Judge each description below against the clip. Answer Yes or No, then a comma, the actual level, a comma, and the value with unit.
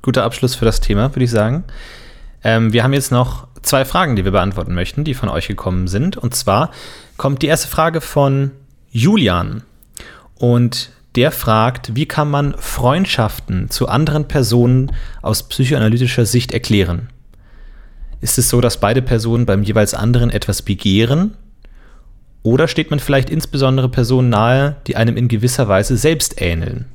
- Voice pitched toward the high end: No, low, 125 Hz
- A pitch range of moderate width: Yes, average, 3.7 semitones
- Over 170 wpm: No, average, 160 wpm